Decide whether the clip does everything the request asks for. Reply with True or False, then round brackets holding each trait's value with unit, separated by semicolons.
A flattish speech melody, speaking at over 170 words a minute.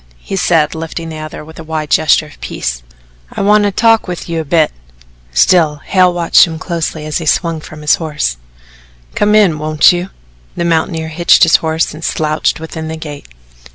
True (2.1 semitones; 190 wpm)